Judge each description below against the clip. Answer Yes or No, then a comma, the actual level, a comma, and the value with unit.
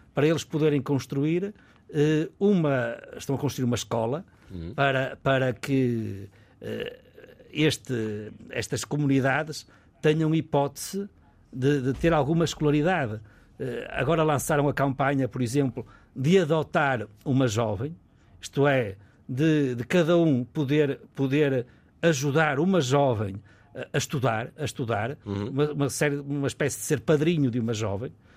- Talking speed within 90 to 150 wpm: Yes, average, 125 wpm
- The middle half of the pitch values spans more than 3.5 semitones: Yes, average, 3.9 semitones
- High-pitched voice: No, medium, 140 Hz